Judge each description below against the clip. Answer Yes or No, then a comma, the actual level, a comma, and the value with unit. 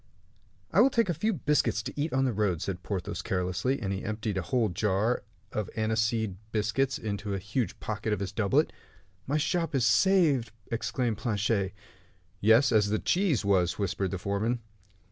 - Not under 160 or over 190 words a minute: Yes, average, 175 wpm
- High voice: No, low, 110 Hz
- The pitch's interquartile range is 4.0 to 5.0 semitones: Yes, average, 4.3 semitones